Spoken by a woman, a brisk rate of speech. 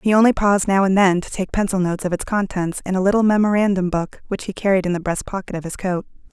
Yes: female; fast, 265 wpm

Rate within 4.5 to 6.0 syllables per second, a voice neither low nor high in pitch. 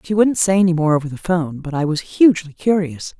No: 6.2 syllables/s; medium, 170 Hz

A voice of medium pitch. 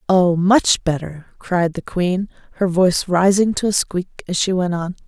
Yes: medium, 180 Hz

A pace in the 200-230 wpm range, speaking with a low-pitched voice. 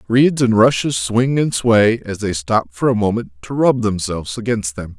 Yes: fast, 205 wpm; low, 110 Hz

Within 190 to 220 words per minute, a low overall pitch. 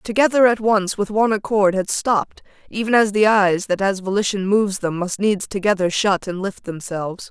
No: average, 195 wpm; high, 200 Hz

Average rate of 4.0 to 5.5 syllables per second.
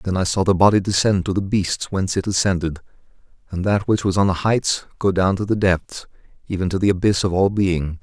No: 5.7 syllables/s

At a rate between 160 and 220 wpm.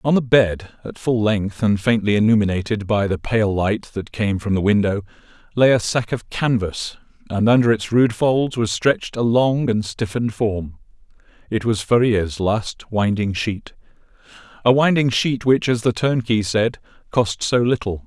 Yes: average, 170 wpm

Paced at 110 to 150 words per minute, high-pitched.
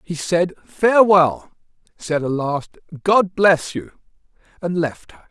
No: slow, 135 wpm; medium, 170 Hz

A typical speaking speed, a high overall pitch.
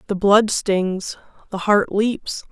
Yes: average, 145 wpm; high, 200 Hz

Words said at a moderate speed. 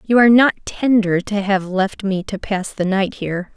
No: fast, 220 wpm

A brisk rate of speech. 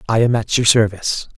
Yes: fast, 215 wpm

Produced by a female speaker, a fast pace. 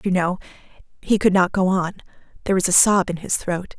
Yes: female; fast, 220 wpm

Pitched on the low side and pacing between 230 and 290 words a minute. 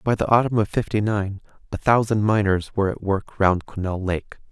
No: low, 100 Hz; average, 200 wpm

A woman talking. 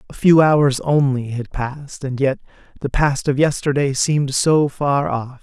No: male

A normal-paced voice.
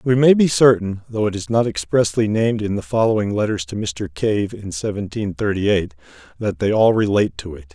No: fast, 210 wpm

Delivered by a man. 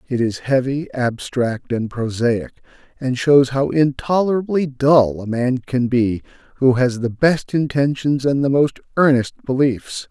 Yes: male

